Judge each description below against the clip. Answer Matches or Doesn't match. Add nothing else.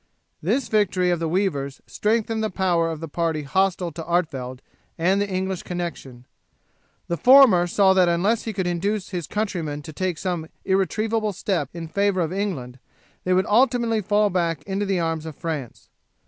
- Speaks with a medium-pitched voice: Matches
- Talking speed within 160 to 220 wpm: Matches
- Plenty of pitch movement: Doesn't match